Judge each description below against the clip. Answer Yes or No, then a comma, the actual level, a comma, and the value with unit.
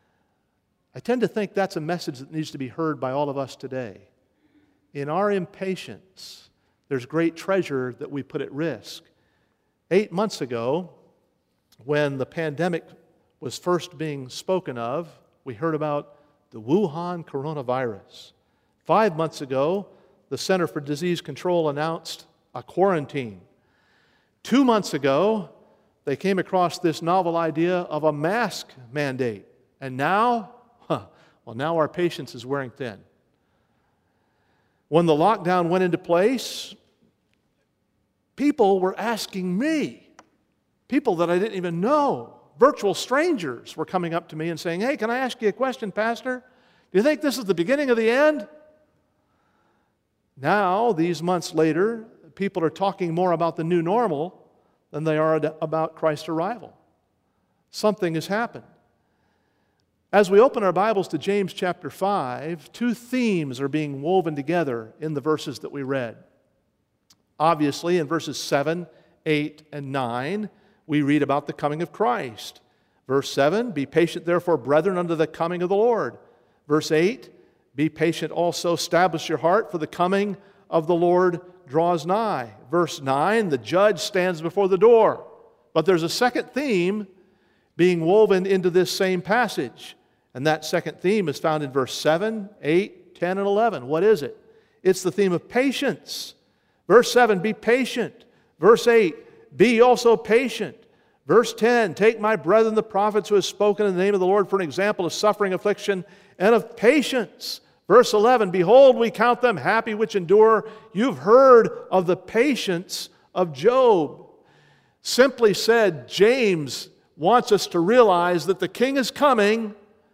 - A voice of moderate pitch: Yes, medium, 180 Hz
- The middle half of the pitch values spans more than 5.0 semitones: Yes, wide, 5.6 semitones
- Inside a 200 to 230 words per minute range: No, average, 155 wpm